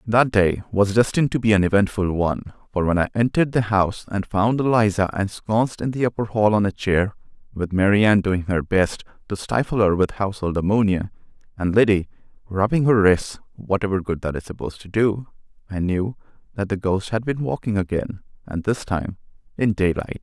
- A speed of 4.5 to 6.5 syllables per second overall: Yes, 5.6 syllables/s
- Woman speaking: No, male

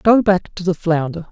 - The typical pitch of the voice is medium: Yes, medium, 180 Hz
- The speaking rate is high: Yes, fast, 230 wpm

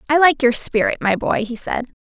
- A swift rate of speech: Yes, fast, 235 wpm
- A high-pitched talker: Yes, very high, 250 Hz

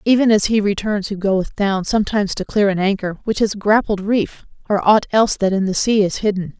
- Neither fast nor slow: No, fast, 225 wpm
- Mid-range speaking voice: No, high, 205 Hz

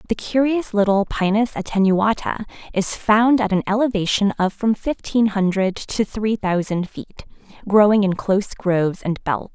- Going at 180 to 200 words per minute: No, average, 150 wpm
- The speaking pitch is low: No, high, 205 Hz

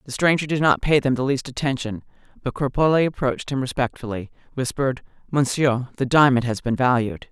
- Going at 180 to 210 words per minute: No, average, 170 wpm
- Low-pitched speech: Yes, low, 130 Hz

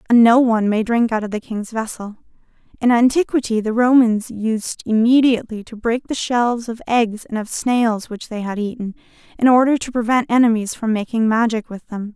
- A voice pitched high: Yes, high, 230 Hz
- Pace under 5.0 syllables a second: No, 5.2 syllables/s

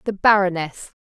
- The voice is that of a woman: Yes, female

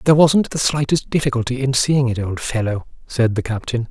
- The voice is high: No, low, 125 Hz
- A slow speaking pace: No, average, 200 wpm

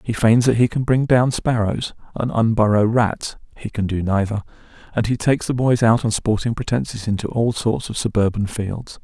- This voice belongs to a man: Yes, male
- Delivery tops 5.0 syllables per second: No, 4.9 syllables/s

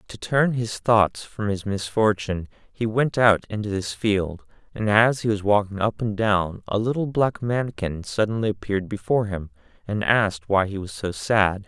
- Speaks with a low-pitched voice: Yes, low, 105 Hz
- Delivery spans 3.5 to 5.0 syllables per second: Yes, 4.8 syllables/s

